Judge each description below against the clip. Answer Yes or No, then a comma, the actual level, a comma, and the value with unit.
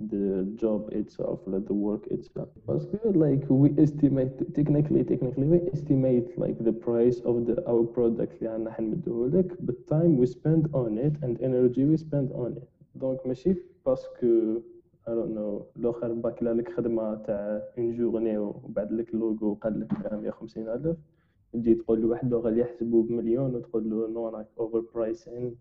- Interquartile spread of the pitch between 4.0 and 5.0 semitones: Yes, average, 4.6 semitones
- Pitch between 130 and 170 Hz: No, low, 120 Hz